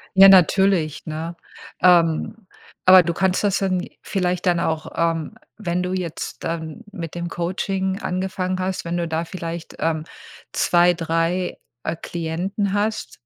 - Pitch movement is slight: Yes, narrow, 2.2 semitones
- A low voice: No, medium, 175 Hz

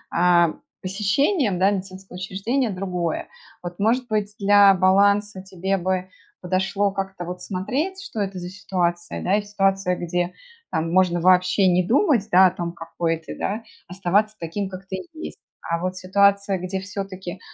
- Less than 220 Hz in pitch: Yes, high, 190 Hz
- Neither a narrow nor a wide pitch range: No, narrow, 2.0 semitones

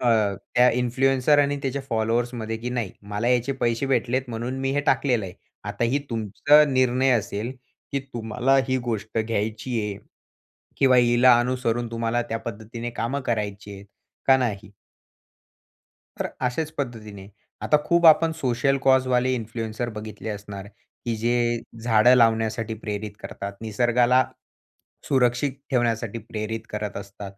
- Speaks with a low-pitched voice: Yes, low, 120 Hz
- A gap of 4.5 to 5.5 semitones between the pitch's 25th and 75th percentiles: No, narrow, 2.6 semitones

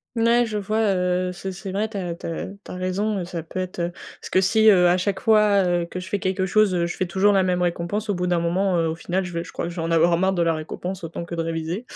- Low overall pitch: No, medium, 185 Hz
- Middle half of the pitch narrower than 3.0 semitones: Yes, narrow, 2.5 semitones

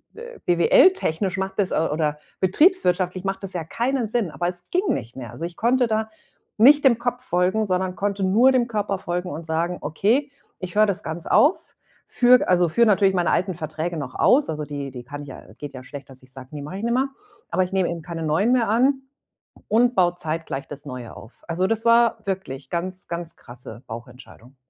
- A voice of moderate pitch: Yes, medium, 180 Hz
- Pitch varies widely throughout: Yes, wide, 6.4 semitones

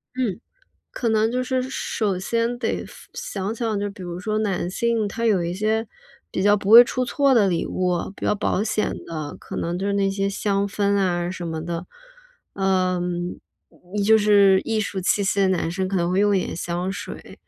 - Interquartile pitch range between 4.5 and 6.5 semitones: No, average, 3.0 semitones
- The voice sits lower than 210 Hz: Yes, high, 200 Hz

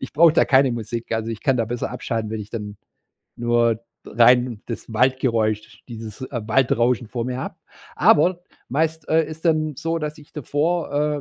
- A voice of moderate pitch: No, low, 125 Hz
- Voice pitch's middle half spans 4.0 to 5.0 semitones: Yes, average, 4.7 semitones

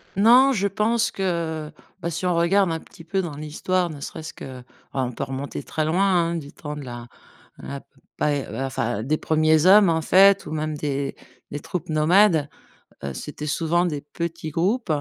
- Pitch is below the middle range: No, medium, 160 Hz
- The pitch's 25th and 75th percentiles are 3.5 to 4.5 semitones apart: Yes, average, 3.8 semitones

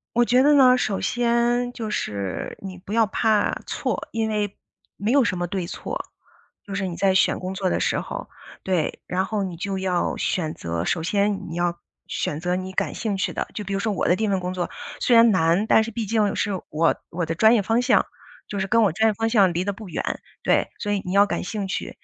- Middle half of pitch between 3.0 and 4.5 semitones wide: Yes, average, 3.5 semitones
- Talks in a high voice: Yes, high, 200 Hz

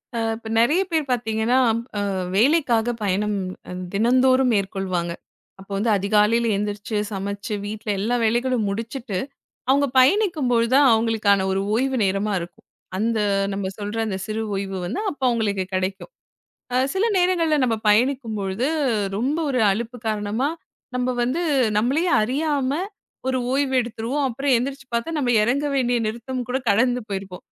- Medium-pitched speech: No, high, 230 Hz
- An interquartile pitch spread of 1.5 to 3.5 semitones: No, average, 4.1 semitones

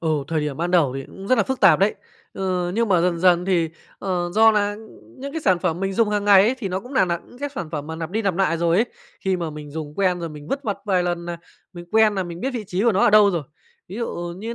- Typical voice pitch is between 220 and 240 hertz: No, medium, 185 Hz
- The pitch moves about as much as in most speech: Yes, average, 3.5 semitones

